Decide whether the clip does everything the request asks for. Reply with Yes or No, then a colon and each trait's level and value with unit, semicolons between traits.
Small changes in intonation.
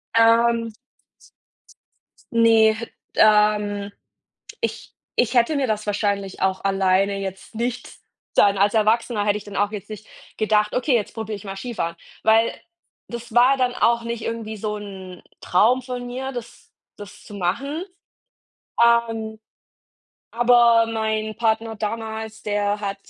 Yes: narrow, 2.2 semitones